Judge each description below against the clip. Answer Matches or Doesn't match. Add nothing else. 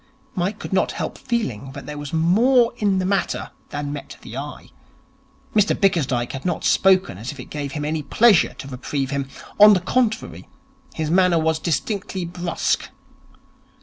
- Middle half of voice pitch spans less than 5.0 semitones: Doesn't match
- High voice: Doesn't match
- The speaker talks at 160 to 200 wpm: Matches